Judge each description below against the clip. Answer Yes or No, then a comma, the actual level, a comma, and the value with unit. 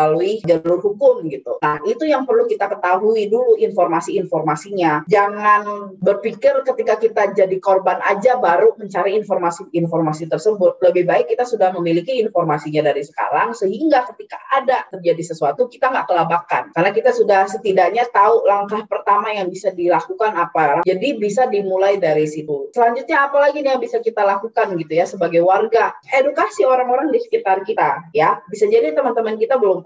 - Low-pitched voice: No, high, 205 Hz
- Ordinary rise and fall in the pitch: No, wide, 6.3 semitones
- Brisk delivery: Yes, fast, 155 wpm